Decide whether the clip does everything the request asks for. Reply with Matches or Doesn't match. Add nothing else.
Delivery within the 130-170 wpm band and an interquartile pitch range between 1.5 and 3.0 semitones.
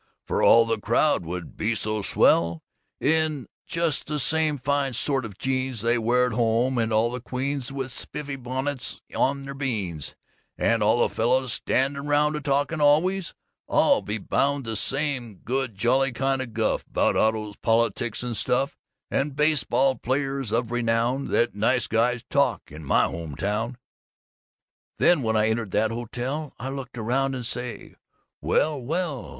Doesn't match